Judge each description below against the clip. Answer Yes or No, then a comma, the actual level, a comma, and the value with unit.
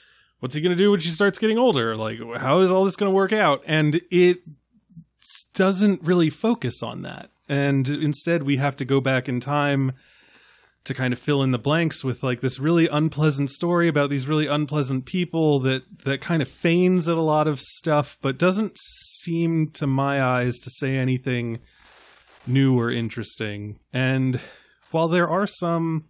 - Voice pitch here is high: No, medium, 150 Hz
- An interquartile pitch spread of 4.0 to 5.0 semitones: Yes, average, 4.4 semitones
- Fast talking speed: No, average, 185 wpm